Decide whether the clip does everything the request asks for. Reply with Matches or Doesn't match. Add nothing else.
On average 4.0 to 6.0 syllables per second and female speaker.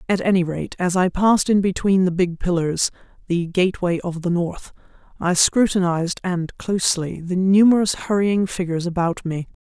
Matches